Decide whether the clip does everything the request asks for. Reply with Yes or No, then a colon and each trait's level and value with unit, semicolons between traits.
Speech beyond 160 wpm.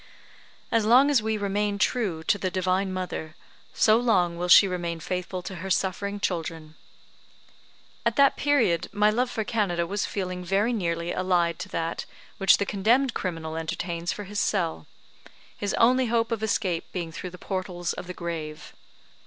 Yes: average, 170 wpm